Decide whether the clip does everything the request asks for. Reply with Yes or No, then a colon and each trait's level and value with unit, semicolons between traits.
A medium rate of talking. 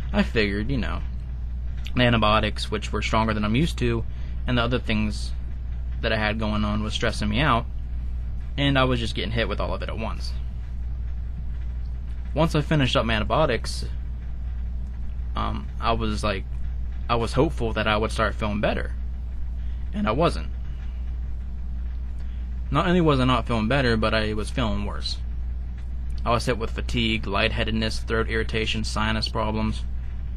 Yes: average, 160 wpm